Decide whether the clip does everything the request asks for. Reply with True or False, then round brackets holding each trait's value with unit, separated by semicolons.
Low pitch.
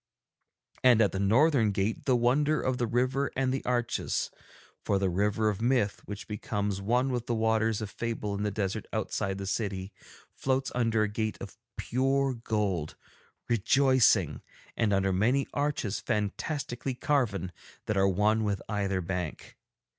True (110 Hz)